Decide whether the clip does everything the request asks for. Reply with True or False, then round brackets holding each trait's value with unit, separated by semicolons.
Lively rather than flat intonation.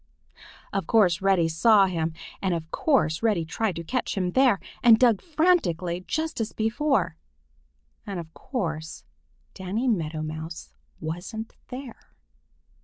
True (6.2 semitones)